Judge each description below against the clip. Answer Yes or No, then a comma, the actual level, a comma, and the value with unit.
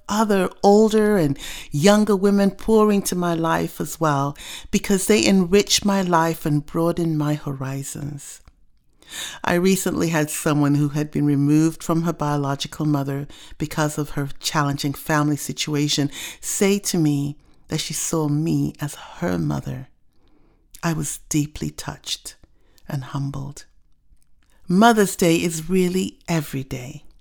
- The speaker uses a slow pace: Yes, slow, 130 wpm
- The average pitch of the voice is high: No, medium, 155 Hz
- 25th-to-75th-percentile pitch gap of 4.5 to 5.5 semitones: No, average, 4.1 semitones